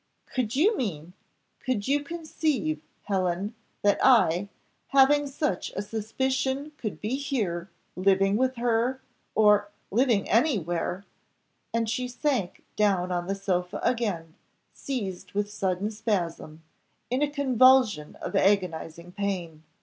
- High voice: Yes, high, 210 Hz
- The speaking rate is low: Yes, slow, 125 wpm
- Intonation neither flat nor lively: No, wide, 6.0 semitones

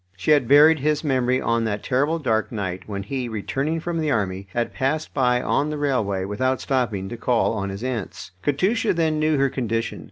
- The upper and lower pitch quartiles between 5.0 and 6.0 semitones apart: Yes, average, 5.3 semitones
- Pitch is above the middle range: No, low, 130 Hz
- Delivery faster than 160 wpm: Yes, average, 200 wpm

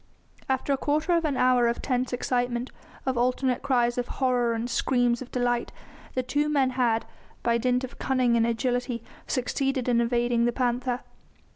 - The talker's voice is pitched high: Yes, very high, 250 Hz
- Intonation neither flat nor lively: No, narrow, 1.4 semitones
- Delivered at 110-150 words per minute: No, average, 170 wpm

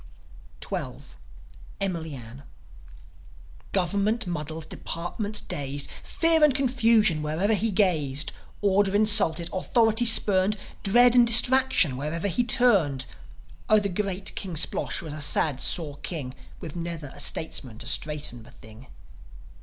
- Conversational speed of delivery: No, slow, 125 wpm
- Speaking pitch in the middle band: Yes, medium, 180 Hz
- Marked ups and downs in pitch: Yes, wide, 6.2 semitones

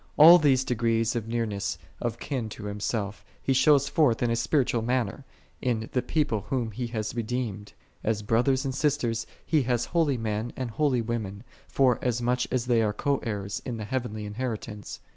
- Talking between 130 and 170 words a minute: No, average, 180 wpm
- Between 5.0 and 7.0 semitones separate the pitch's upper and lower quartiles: No, average, 3.0 semitones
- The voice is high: No, low, 120 Hz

